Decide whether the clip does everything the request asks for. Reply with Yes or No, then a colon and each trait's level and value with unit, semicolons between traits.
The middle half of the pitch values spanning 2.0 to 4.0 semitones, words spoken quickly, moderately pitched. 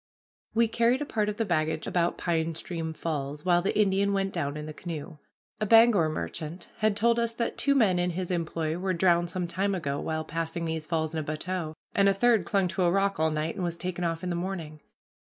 Yes: average, 3.6 semitones; fast, 230 wpm; medium, 175 Hz